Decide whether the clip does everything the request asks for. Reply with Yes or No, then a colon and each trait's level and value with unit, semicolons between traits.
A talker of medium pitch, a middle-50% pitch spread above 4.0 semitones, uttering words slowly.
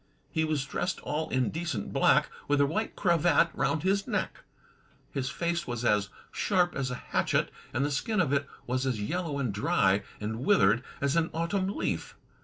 No: medium, 145 Hz; average, 5.3 semitones; average, 190 wpm